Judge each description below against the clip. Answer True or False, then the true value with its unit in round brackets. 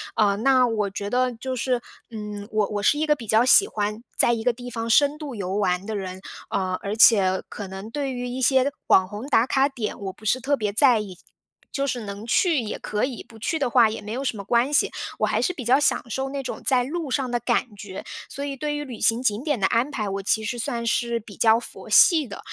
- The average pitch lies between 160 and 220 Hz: False (235 Hz)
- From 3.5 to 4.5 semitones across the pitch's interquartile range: True (4.1 semitones)